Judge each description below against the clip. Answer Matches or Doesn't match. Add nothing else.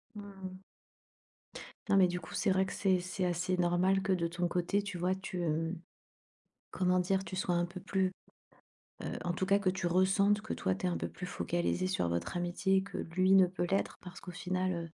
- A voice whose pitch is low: Doesn't match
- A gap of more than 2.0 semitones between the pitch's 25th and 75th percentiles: Doesn't match